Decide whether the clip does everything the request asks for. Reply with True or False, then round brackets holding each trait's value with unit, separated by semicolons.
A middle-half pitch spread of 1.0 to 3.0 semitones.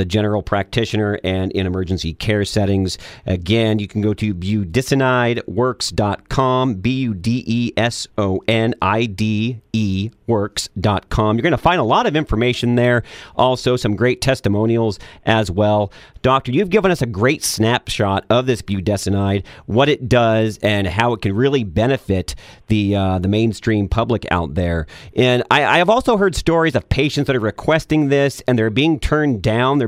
False (3.8 semitones)